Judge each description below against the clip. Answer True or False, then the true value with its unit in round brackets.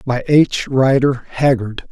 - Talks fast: False (125 wpm)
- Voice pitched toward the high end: False (130 Hz)